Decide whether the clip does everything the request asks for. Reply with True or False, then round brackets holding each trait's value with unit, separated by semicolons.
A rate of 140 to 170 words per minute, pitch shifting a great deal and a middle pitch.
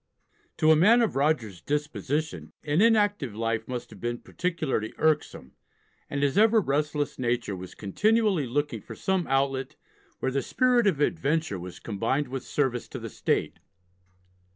True (155 wpm; 5.8 semitones; 145 Hz)